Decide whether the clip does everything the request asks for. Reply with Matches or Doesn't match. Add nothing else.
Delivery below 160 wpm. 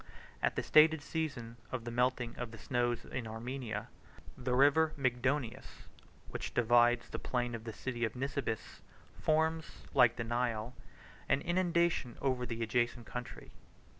Matches